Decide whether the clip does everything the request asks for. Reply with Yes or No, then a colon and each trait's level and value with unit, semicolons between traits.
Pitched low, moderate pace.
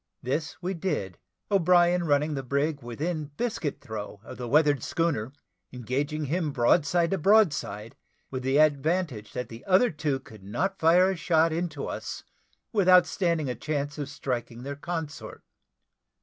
No: medium, 150 Hz; average, 150 wpm